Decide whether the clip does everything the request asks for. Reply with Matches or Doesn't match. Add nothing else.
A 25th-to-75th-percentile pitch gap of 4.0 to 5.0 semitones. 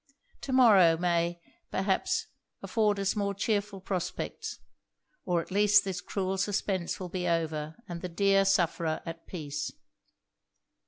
Doesn't match